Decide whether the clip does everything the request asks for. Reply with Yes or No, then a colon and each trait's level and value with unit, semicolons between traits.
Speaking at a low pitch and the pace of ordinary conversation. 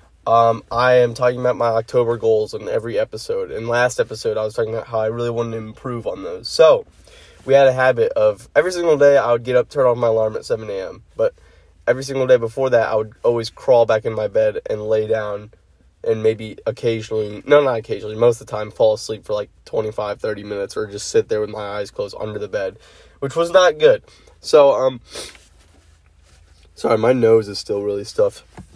No: low, 130 Hz; fast, 215 wpm